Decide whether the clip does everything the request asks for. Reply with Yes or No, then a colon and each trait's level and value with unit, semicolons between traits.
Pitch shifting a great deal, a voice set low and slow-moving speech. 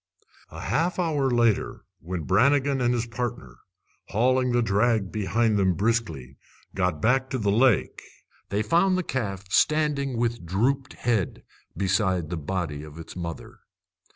No: wide, 5.7 semitones; low, 115 Hz; average, 145 wpm